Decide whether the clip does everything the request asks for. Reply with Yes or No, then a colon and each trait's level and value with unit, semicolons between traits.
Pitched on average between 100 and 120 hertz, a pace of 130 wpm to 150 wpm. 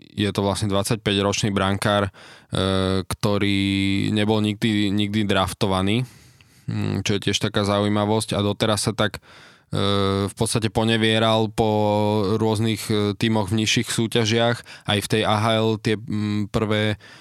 No: low, 105 Hz; average, 120 wpm